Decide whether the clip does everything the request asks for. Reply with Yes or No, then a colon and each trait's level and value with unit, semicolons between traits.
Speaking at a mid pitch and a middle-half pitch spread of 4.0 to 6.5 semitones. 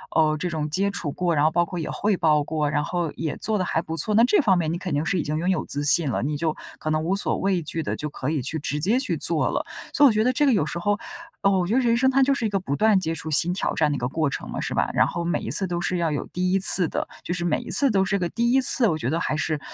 Yes: medium, 175 Hz; average, 4.4 semitones